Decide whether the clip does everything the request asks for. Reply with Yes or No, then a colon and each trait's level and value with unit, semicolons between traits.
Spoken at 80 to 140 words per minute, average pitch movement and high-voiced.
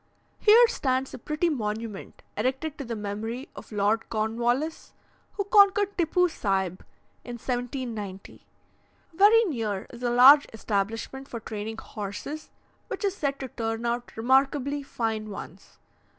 Yes: slow, 135 wpm; average, 5.0 semitones; high, 245 Hz